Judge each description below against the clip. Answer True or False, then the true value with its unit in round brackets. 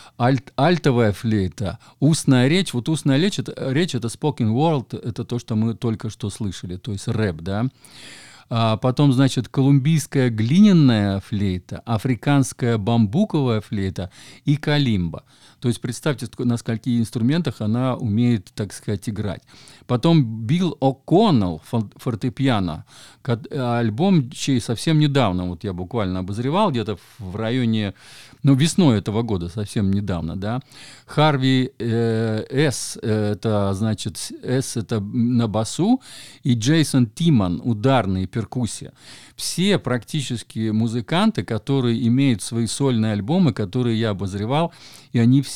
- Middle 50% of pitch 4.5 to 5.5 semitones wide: False (3.8 semitones)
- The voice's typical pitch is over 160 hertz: False (120 Hz)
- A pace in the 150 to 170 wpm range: False (130 wpm)